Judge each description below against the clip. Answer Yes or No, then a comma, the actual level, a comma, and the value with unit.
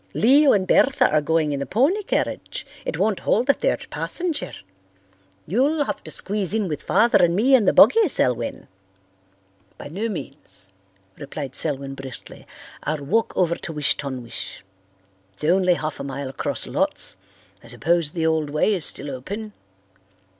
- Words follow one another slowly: No, average, 165 wpm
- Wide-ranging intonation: Yes, wide, 7.7 semitones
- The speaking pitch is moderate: Yes, medium, 170 Hz